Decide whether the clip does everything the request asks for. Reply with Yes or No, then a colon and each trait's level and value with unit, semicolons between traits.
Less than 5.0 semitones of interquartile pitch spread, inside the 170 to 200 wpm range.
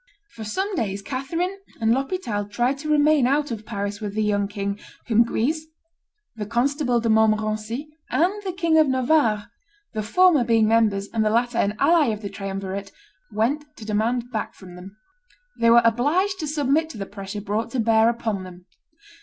No: average, 5.3 semitones; average, 180 wpm